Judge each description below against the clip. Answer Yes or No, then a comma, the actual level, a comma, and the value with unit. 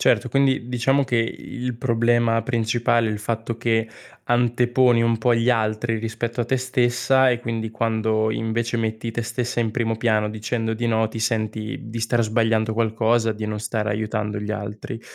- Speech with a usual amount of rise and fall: No, narrow, 1.5 semitones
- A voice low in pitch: Yes, low, 115 Hz